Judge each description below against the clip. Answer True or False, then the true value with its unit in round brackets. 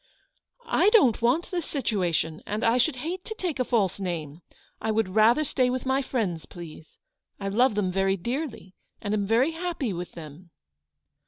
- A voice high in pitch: True (225 Hz)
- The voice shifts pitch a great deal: True (6.5 semitones)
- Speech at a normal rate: True (180 wpm)